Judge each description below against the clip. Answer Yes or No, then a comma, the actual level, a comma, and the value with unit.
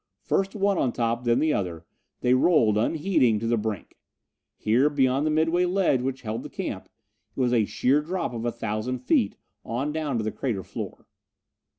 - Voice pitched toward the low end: Yes, low, 125 Hz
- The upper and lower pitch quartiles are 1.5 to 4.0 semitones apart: No, average, 5.0 semitones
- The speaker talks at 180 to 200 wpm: Yes, average, 190 wpm